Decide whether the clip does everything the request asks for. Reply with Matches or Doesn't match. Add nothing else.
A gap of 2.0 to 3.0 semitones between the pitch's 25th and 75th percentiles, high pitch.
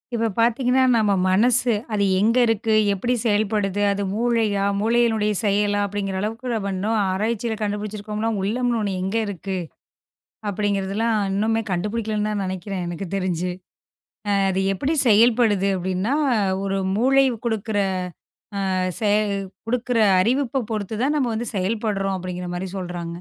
Matches